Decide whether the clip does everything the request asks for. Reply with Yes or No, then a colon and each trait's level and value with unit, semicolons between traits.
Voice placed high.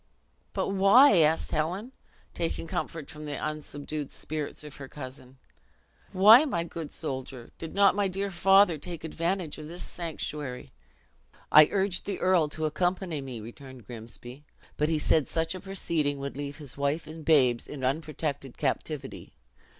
No: medium, 155 Hz